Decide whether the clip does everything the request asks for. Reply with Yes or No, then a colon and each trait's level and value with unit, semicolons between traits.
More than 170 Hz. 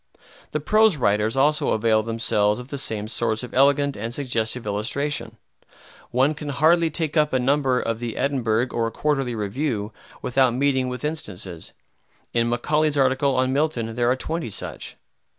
No: low, 125 Hz